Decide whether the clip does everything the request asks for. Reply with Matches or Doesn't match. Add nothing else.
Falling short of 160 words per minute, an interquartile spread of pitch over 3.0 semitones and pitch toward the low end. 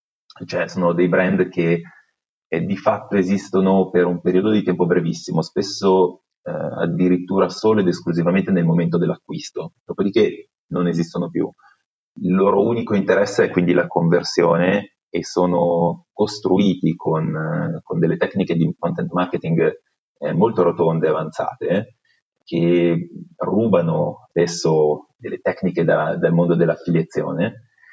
Doesn't match